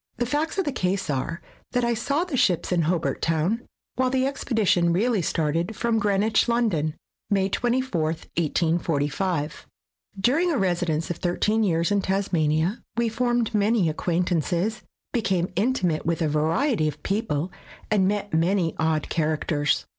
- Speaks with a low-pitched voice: No, high, 190 Hz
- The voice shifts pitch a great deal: Yes, wide, 5.9 semitones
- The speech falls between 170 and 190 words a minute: No, average, 145 wpm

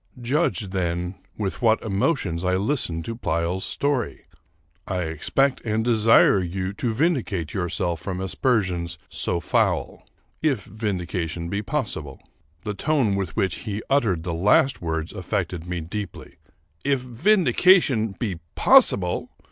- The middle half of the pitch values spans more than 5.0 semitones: Yes, wide, 5.5 semitones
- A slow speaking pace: Yes, slow, 130 wpm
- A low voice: Yes, low, 100 Hz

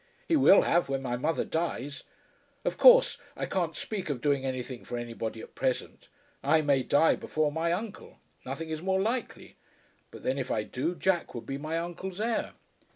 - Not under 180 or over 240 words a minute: Yes, average, 185 wpm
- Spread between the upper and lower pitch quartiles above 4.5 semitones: Yes, average, 5.2 semitones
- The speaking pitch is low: No, medium, 155 Hz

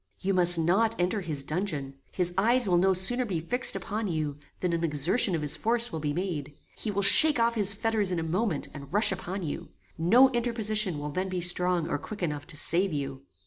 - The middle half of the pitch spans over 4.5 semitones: Yes, average, 5.2 semitones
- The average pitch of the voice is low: No, medium, 180 Hz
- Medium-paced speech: No, fast, 220 wpm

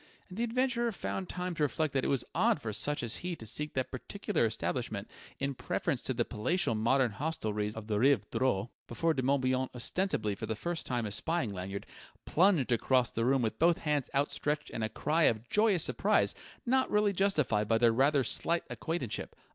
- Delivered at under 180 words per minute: No, average, 195 wpm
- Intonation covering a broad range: Yes, wide, 6.9 semitones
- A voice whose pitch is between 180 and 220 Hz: No, low, 135 Hz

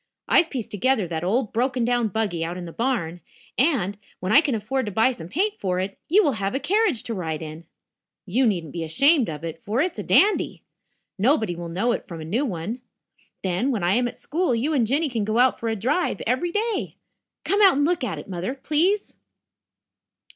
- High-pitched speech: Yes, high, 230 Hz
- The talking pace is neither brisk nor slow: No, fast, 220 wpm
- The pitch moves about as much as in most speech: No, wide, 7.2 semitones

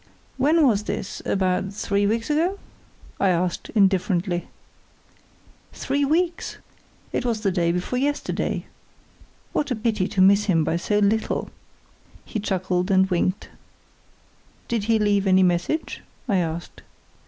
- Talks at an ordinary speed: No, slow, 130 wpm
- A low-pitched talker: No, high, 200 Hz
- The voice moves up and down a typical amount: Yes, average, 3.9 semitones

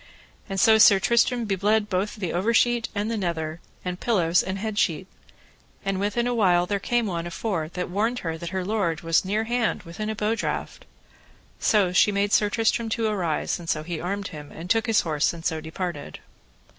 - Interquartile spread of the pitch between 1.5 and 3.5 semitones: No, average, 4.1 semitones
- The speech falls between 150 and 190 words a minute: No, fast, 205 wpm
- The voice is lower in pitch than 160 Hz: No, high, 195 Hz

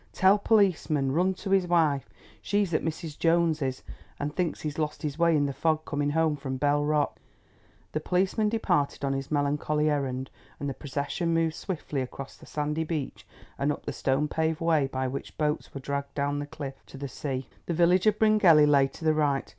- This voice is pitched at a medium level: Yes, medium, 150 Hz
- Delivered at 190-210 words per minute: Yes, average, 200 wpm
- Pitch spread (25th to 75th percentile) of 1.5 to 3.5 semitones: Yes, average, 2.9 semitones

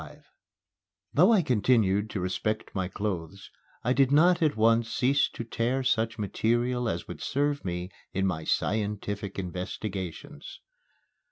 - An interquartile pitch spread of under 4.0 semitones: No, average, 4.9 semitones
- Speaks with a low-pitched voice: Yes, low, 110 Hz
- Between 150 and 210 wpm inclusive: No, average, 140 wpm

